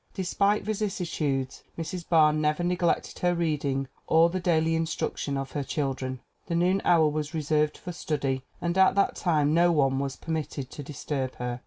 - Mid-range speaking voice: Yes, medium, 155 Hz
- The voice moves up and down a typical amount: Yes, average, 3.8 semitones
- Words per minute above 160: Yes, average, 170 wpm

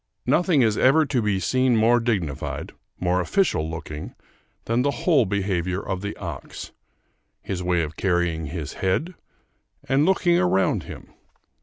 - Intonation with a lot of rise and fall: Yes, wide, 6.9 semitones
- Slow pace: No, average, 145 wpm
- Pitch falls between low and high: No, low, 100 Hz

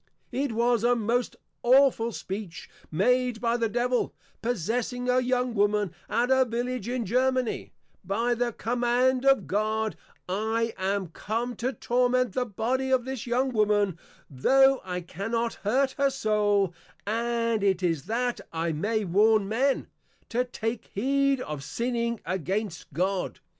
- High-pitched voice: Yes, high, 230 Hz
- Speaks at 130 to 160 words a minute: Yes, average, 140 wpm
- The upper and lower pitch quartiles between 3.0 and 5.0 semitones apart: Yes, average, 3.4 semitones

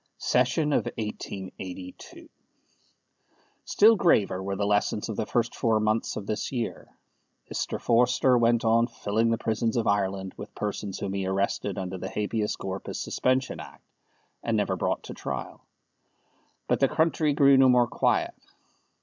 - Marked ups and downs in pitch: No, average, 3.6 semitones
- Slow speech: No, average, 150 wpm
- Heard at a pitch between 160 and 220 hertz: No, low, 110 Hz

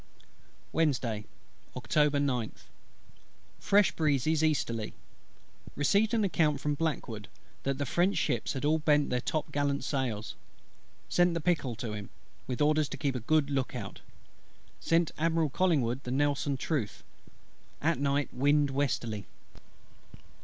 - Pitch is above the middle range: No, medium, 145 Hz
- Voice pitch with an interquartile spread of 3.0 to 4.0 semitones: Yes, average, 3.7 semitones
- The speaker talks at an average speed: No, slow, 130 wpm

